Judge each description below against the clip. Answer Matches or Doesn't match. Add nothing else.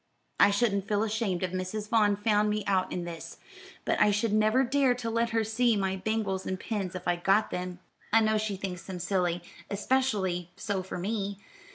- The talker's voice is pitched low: Doesn't match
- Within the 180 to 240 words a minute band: Matches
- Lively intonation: Doesn't match